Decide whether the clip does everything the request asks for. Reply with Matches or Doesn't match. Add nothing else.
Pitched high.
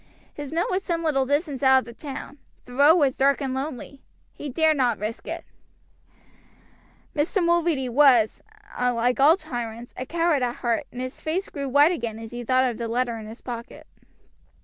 Matches